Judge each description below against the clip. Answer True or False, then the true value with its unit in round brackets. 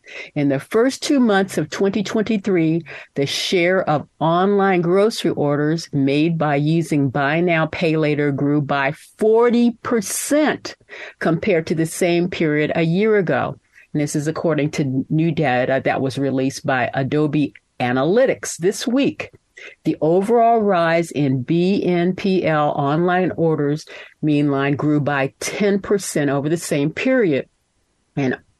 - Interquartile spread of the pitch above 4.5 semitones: True (5.2 semitones)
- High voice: False (165 Hz)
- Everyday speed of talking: False (130 wpm)